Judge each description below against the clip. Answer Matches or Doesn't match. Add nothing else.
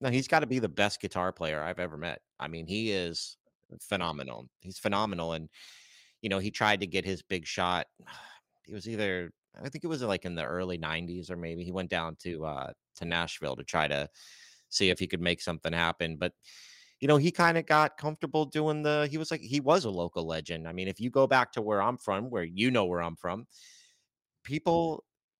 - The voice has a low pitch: Matches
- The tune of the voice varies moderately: Doesn't match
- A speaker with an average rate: Doesn't match